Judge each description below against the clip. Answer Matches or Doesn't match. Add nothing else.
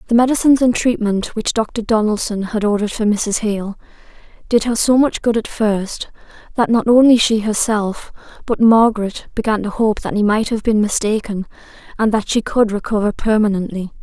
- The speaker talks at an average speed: Matches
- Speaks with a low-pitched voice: Doesn't match